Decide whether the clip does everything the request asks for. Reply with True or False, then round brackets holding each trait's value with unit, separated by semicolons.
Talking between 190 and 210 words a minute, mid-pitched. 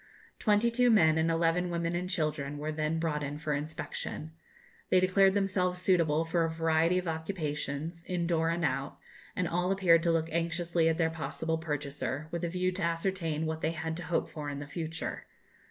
True (195 wpm; 165 Hz)